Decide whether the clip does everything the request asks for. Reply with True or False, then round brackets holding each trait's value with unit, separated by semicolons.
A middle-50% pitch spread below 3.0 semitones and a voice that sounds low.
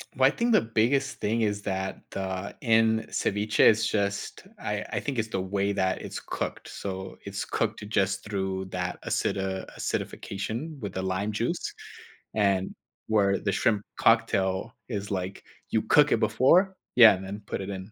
True (2.6 semitones; 100 Hz)